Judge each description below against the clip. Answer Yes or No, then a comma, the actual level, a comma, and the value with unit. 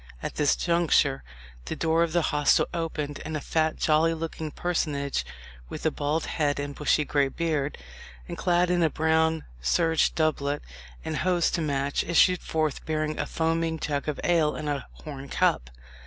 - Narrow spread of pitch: Yes, narrow, 2.1 semitones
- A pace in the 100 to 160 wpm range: No, average, 170 wpm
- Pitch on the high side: No, medium, 155 Hz